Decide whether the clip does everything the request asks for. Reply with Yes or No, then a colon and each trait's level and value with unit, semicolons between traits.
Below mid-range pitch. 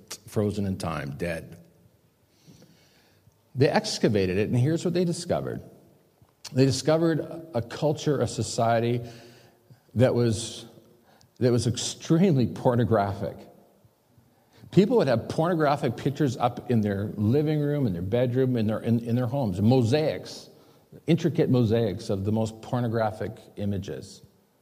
Yes: low, 120 Hz